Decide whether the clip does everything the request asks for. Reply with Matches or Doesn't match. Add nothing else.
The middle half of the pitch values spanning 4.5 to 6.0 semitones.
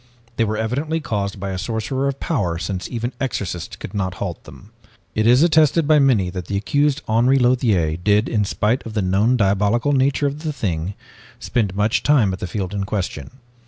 Matches